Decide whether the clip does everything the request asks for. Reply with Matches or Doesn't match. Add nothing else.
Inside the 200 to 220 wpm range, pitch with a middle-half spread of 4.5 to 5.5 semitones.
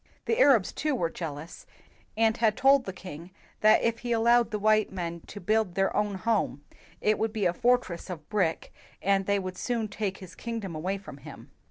Doesn't match